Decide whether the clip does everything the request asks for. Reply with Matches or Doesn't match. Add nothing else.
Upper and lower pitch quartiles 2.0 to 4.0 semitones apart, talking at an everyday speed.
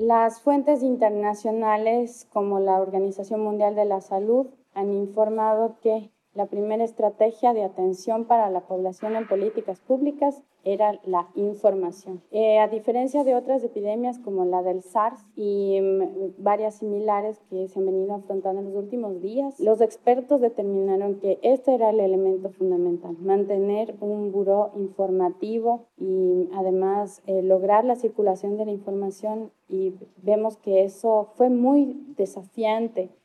Matches